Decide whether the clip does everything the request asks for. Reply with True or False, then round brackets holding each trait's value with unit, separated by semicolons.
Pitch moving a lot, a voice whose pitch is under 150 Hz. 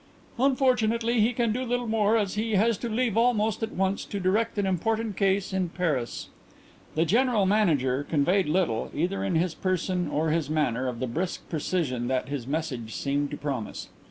False (6.8 semitones; 185 Hz)